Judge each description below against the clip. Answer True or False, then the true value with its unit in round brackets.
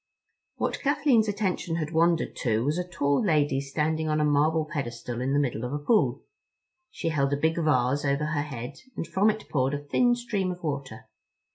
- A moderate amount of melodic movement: True (3.7 semitones)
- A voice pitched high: False (150 Hz)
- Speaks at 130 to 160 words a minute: False (195 wpm)